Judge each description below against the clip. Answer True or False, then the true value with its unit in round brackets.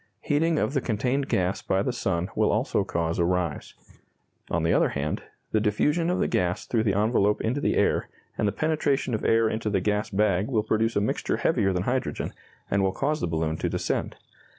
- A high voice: False (105 Hz)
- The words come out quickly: True (210 wpm)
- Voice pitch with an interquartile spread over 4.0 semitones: True (5.4 semitones)